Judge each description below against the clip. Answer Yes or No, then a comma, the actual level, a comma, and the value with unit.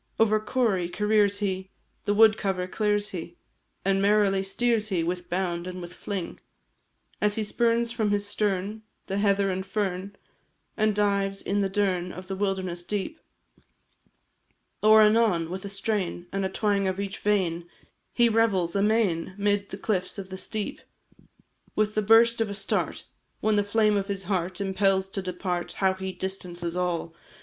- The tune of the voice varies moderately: No, narrow, 2.1 semitones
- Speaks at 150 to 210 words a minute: Yes, average, 165 wpm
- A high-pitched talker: Yes, high, 195 Hz